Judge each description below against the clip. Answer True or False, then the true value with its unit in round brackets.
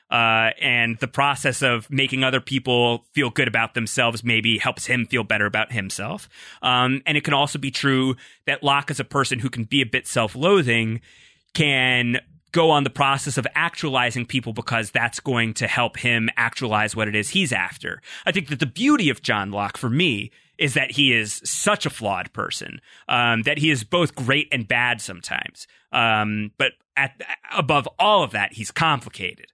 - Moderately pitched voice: False (125 Hz)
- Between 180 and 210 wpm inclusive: True (190 wpm)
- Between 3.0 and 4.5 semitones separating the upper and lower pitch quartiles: True (3.6 semitones)